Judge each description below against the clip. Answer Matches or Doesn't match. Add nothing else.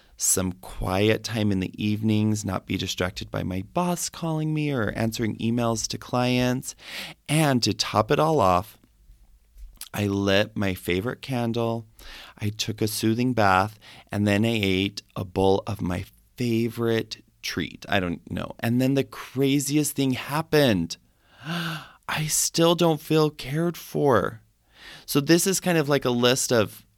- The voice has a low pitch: Matches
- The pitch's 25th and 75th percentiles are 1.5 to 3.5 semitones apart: Doesn't match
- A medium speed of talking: Matches